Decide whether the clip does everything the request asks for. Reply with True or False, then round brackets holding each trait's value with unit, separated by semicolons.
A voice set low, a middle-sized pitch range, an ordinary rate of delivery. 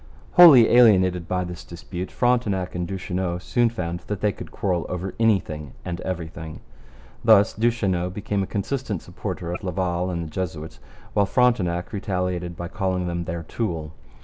True (90 Hz; 3.1 semitones; 155 wpm)